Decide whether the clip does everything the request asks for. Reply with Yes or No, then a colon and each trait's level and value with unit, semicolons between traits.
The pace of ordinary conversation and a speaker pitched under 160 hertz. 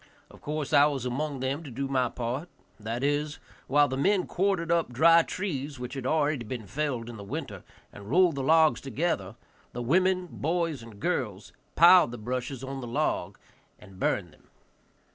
Yes: average, 180 wpm; medium, 140 Hz